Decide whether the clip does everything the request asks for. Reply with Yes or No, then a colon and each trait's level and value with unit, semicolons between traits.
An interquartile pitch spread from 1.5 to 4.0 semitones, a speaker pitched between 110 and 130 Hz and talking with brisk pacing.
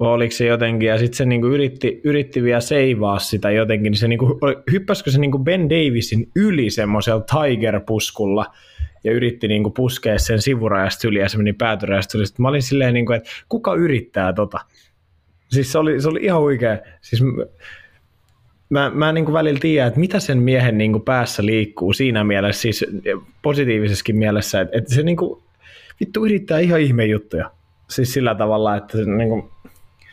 No: average, 4.7 semitones; low, 115 Hz; fast, 170 wpm